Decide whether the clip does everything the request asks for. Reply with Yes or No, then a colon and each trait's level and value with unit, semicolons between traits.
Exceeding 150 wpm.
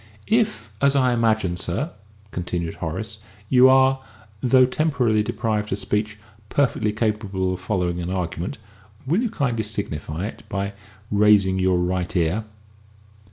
No: slow, 135 wpm